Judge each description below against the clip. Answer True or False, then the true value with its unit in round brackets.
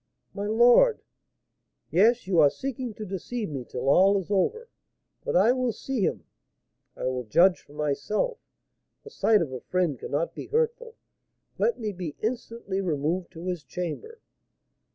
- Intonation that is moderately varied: False (7.0 semitones)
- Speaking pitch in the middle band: False (195 Hz)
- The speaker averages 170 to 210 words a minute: False (160 wpm)